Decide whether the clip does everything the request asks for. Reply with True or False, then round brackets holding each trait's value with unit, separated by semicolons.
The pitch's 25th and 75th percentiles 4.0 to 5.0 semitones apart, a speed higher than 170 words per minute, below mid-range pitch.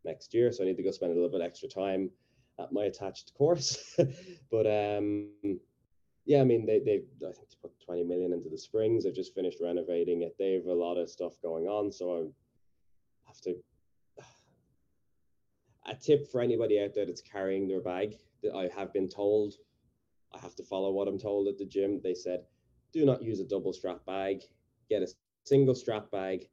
True (4.6 semitones; 205 wpm; 100 Hz)